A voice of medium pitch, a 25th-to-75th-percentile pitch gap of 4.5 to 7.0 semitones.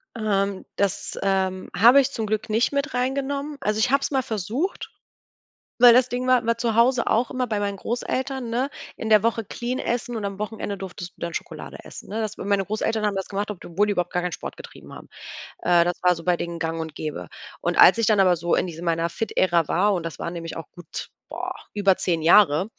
No: high, 205 Hz; average, 4.8 semitones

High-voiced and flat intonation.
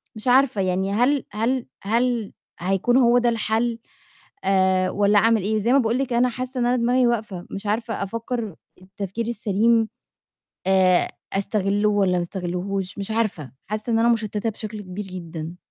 No: high, 215 Hz; average, 3.5 semitones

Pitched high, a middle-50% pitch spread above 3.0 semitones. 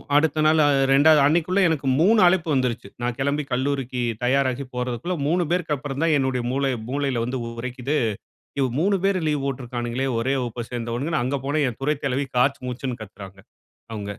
No: low, 135 Hz; average, 3.5 semitones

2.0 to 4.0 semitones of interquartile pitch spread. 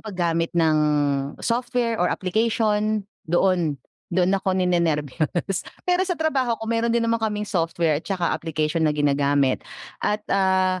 No: average, 5.1 semitones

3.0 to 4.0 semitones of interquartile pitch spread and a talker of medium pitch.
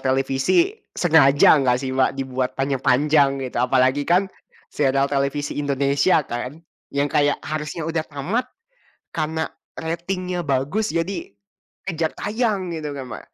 Yes: average, 3.7 semitones; medium, 145 Hz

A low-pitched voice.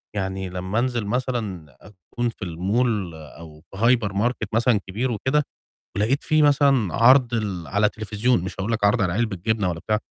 Yes: low, 105 Hz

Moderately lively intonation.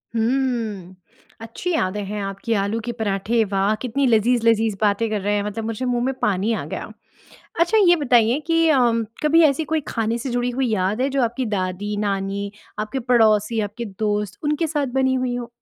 Yes: average, 3.8 semitones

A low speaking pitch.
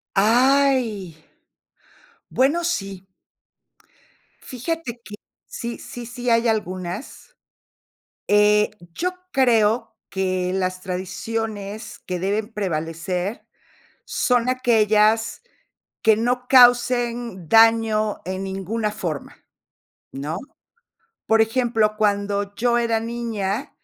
No: high, 220 Hz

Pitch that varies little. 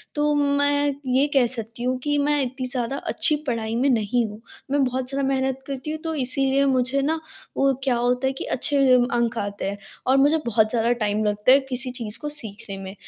No: average, 3.2 semitones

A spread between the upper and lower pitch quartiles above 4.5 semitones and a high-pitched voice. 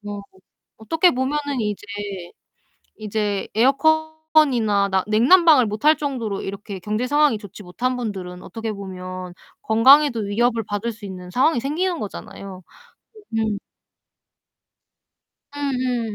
Yes: wide, 5.4 semitones; high, 225 Hz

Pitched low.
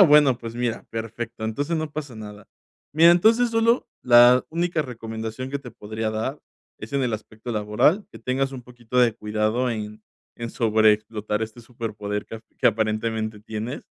Yes: low, 115 Hz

